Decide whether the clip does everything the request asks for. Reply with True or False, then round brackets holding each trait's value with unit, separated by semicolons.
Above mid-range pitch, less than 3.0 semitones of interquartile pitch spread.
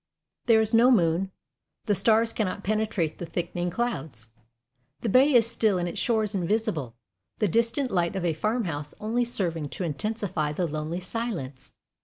False (195 Hz; 5.3 semitones)